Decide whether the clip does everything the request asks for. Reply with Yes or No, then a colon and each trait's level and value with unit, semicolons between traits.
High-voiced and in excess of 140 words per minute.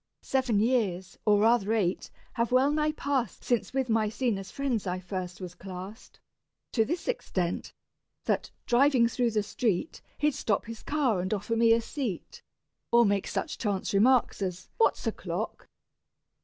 Yes: high, 225 Hz; average, 155 wpm